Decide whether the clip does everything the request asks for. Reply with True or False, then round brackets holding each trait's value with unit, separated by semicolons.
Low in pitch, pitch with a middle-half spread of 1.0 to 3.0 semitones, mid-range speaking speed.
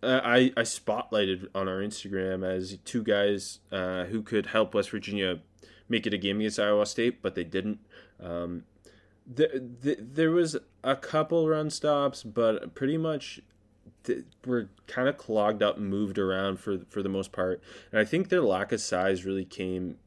False (105 Hz; 4.2 semitones; 180 wpm)